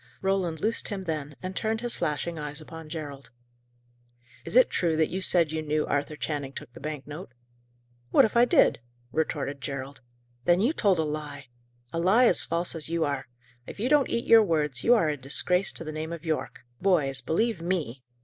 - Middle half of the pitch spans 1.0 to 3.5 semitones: No, average, 4.2 semitones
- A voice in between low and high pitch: Yes, medium, 160 Hz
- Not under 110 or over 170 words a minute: No, average, 200 wpm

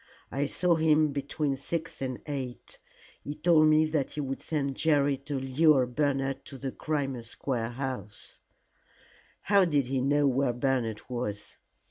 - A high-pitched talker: No, medium, 140 Hz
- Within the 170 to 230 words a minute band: No, average, 155 wpm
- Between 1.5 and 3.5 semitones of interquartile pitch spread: Yes, average, 2.7 semitones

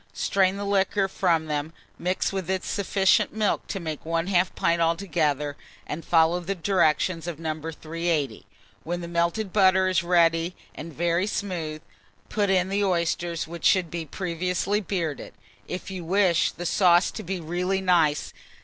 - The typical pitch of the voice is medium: Yes, medium, 175 Hz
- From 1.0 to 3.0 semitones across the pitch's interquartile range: Yes, narrow, 2.5 semitones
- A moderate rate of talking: Yes, average, 160 wpm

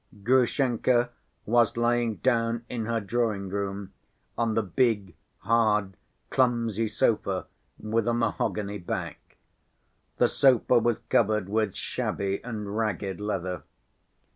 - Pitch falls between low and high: No, low, 110 Hz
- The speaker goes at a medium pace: No, slow, 110 wpm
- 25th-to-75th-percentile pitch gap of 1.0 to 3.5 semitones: Yes, average, 2.7 semitones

